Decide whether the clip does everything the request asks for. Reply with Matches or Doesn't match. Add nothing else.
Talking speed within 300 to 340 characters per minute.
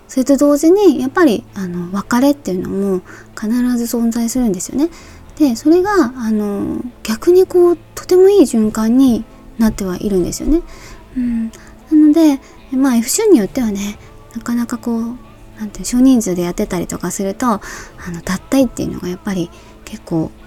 Matches